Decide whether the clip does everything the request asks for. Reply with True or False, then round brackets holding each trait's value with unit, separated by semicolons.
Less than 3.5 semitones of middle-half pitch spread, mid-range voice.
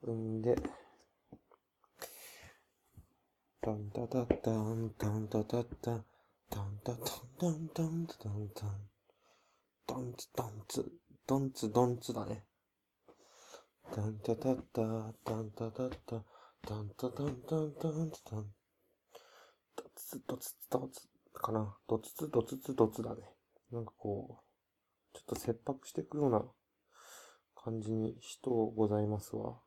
False (2.7 semitones; 115 Hz)